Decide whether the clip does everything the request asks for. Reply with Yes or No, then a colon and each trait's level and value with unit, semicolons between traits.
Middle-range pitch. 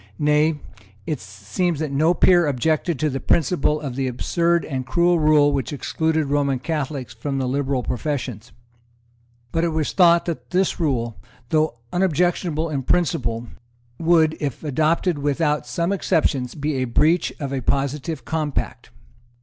Yes: medium, 150 Hz